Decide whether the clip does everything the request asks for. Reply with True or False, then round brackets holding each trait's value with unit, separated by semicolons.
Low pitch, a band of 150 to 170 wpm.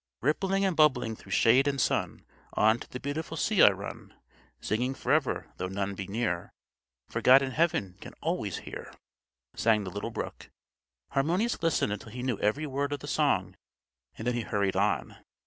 False (125 Hz; 180 wpm)